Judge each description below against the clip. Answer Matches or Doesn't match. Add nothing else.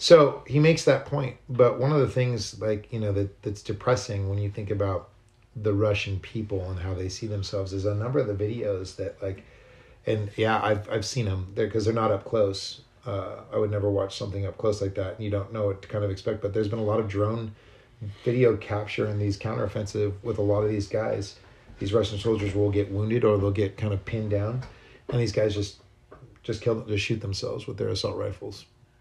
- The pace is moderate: Doesn't match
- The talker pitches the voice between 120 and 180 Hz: Doesn't match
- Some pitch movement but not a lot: Doesn't match